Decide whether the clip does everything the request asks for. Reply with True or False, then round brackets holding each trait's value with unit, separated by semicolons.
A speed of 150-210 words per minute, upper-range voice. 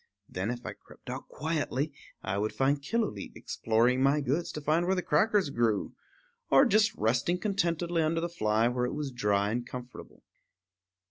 False (175 wpm; 140 Hz)